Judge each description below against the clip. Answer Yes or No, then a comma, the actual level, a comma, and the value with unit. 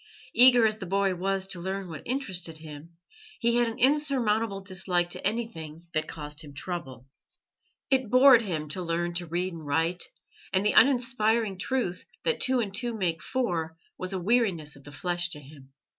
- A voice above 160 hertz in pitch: Yes, medium, 185 Hz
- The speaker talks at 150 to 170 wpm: No, average, 180 wpm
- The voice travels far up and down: Yes, wide, 5.8 semitones